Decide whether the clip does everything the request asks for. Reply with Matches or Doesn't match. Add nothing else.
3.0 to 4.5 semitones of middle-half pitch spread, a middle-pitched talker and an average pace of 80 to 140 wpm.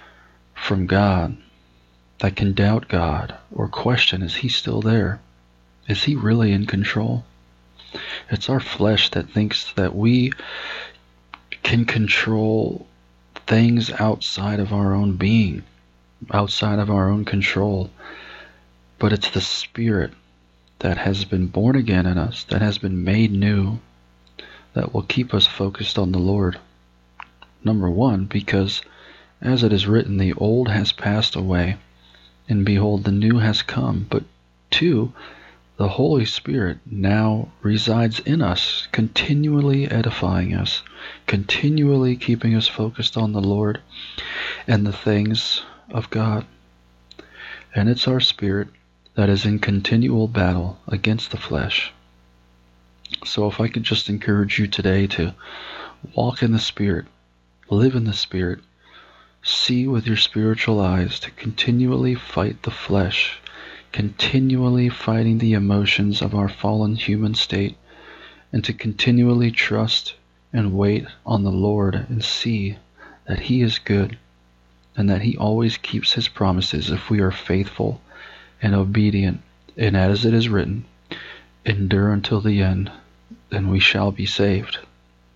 Doesn't match